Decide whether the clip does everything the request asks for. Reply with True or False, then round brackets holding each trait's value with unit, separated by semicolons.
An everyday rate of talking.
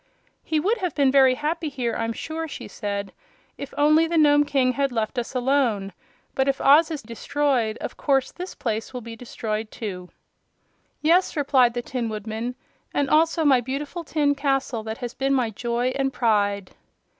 True (180 wpm)